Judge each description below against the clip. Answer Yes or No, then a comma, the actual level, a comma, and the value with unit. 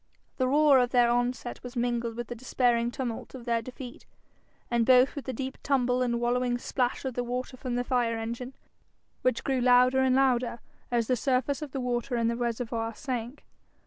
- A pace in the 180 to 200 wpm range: Yes, average, 195 wpm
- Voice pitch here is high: Yes, high, 245 Hz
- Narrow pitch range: Yes, narrow, 1.4 semitones